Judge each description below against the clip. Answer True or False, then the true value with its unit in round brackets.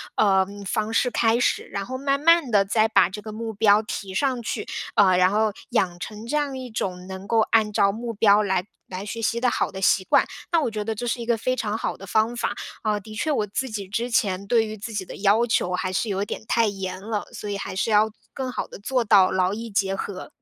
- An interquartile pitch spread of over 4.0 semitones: False (2.7 semitones)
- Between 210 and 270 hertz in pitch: True (215 Hz)